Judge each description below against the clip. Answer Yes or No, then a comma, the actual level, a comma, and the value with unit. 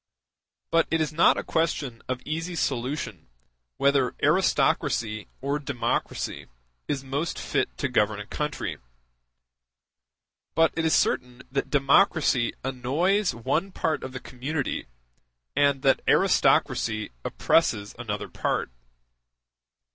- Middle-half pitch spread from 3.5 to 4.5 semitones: Yes, average, 4.1 semitones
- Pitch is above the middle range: No, low, 135 Hz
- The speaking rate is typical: No, slow, 110 wpm